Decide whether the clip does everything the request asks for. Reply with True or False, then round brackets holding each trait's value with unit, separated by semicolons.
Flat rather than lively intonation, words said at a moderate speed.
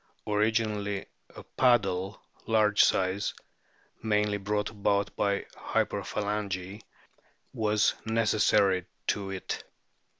False (1.4 semitones; 80 wpm)